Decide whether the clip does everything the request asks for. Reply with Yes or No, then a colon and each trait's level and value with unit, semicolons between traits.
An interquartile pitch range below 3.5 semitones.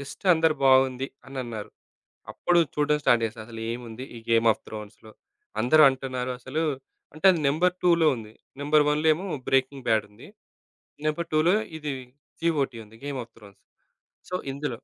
No: average, 4.9 semitones